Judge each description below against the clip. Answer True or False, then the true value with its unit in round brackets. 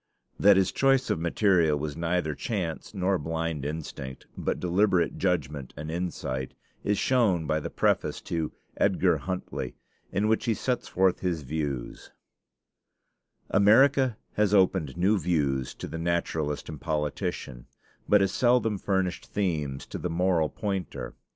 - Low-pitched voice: True (85 Hz)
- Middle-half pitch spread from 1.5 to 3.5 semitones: False (4.3 semitones)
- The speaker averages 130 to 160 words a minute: True (140 wpm)